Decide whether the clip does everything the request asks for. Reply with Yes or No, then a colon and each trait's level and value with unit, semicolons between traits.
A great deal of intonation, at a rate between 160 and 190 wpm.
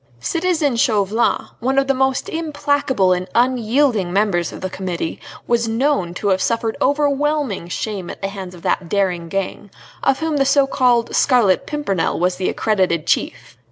Yes: wide, 6.5 semitones; average, 165 wpm